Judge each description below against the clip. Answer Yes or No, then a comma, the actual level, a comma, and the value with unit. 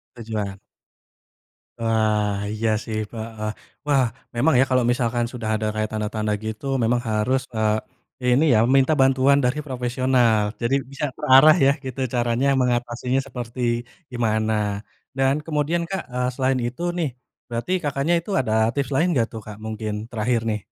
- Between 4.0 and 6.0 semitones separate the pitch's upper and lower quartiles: No, average, 3.4 semitones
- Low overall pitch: Yes, low, 120 Hz